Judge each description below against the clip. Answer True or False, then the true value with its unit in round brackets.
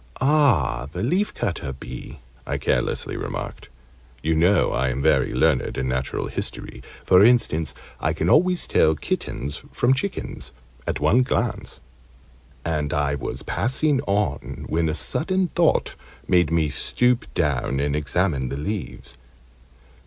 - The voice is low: True (80 Hz)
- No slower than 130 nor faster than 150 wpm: True (135 wpm)